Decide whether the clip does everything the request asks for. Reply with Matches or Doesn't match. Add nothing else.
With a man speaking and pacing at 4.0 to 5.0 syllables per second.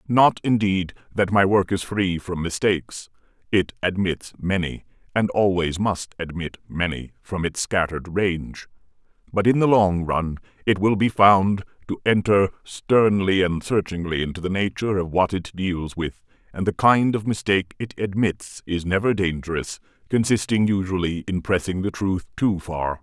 Matches